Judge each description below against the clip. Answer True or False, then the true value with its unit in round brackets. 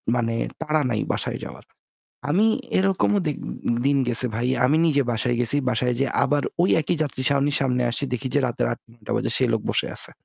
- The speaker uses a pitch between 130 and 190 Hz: True (135 Hz)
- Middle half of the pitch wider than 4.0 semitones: False (3.6 semitones)